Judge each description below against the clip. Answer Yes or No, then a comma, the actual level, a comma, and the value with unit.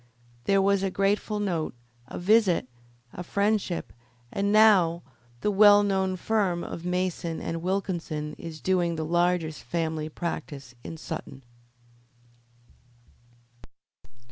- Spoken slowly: Yes, slow, 115 wpm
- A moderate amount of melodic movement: Yes, average, 3.3 semitones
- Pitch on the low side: No, medium, 180 Hz